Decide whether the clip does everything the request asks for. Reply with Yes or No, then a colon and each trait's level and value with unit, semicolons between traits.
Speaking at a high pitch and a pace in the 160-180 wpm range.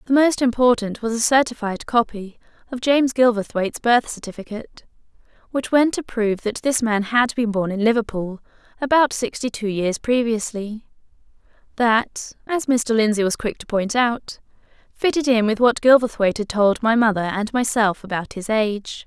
Yes: high, 225 Hz; average, 165 wpm